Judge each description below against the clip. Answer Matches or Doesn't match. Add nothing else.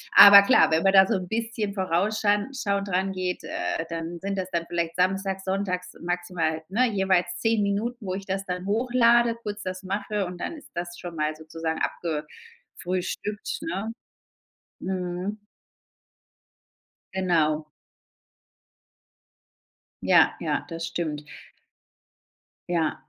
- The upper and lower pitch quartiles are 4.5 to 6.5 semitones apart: Doesn't match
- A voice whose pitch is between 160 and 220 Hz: Matches